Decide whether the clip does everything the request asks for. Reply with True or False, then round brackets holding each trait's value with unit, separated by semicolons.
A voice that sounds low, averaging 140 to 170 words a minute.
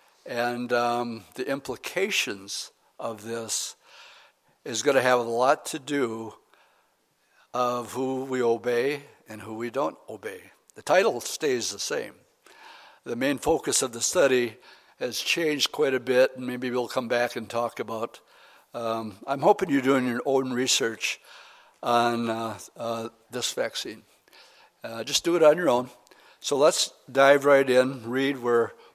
True (125 Hz; 155 wpm)